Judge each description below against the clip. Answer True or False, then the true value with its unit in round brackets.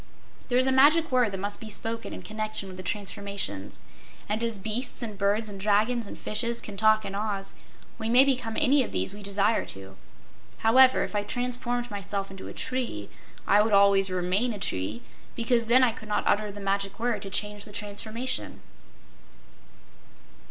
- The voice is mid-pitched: False (210 Hz)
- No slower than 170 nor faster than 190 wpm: True (180 wpm)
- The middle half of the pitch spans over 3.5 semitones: False (3.0 semitones)